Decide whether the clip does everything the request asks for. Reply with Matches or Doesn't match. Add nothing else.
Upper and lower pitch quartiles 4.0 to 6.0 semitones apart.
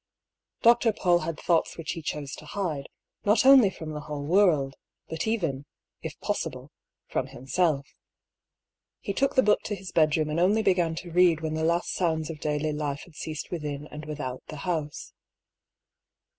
Doesn't match